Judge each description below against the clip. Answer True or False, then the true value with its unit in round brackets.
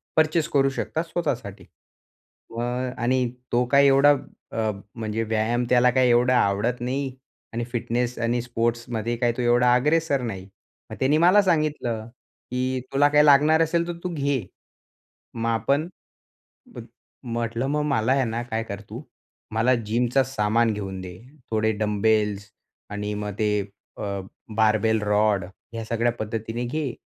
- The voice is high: False (120 Hz)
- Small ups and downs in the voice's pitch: False (3.5 semitones)